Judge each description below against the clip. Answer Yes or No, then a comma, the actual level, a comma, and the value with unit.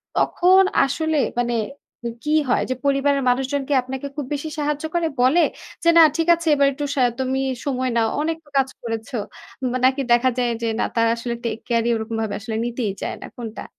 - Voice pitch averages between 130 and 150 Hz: No, very high, 260 Hz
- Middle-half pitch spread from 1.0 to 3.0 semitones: No, average, 3.6 semitones